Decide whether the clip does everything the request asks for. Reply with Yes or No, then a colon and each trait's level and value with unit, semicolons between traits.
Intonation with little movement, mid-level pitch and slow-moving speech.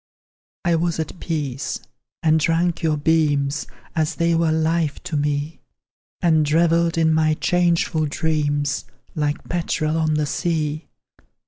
Yes: narrow, 1.8 semitones; medium, 160 Hz; slow, 130 wpm